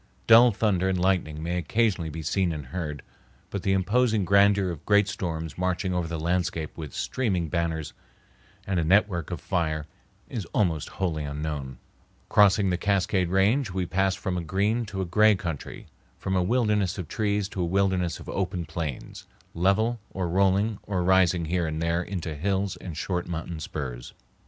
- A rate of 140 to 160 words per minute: No, average, 175 wpm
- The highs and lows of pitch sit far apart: No, average, 3.2 semitones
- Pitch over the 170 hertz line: No, very low, 90 Hz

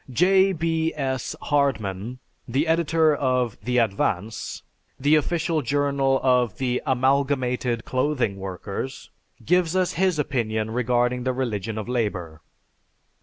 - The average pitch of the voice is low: Yes, low, 130 Hz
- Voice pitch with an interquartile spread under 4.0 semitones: No, average, 4.3 semitones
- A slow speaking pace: Yes, slow, 120 wpm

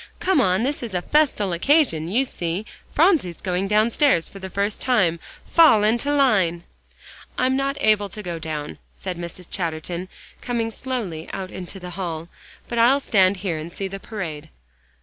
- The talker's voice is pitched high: Yes, high, 195 Hz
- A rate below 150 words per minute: No, average, 170 wpm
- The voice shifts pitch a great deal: Yes, wide, 5.8 semitones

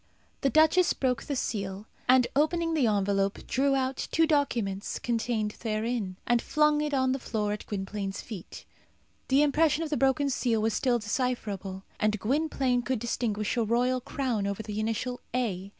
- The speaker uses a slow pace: No, average, 165 wpm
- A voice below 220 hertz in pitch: No, high, 240 Hz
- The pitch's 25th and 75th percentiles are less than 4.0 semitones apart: No, average, 4.4 semitones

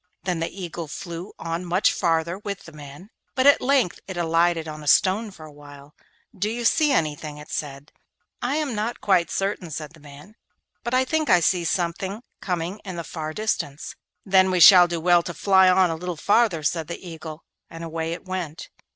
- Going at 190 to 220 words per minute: Yes, fast, 205 wpm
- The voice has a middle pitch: Yes, medium, 175 Hz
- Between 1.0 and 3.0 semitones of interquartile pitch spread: No, average, 3.4 semitones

